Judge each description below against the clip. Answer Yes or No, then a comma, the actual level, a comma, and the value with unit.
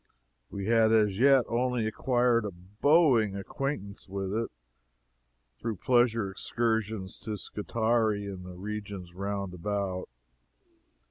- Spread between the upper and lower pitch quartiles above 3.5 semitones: No, average, 3.0 semitones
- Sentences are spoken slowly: Yes, slow, 115 wpm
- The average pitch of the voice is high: No, low, 105 Hz